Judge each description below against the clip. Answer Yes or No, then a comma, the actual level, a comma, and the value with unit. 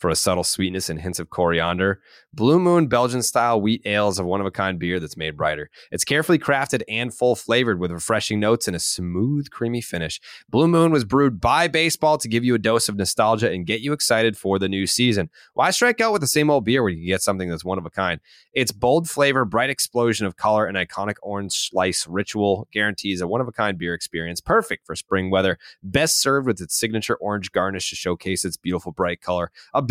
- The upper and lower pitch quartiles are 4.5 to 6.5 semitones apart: Yes, average, 5.3 semitones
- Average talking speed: No, fast, 225 wpm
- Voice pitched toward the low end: Yes, low, 105 Hz